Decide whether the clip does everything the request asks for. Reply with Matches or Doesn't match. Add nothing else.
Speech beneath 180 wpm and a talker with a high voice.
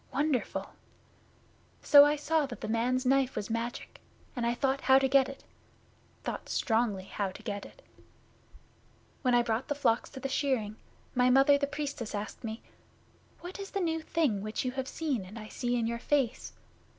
Doesn't match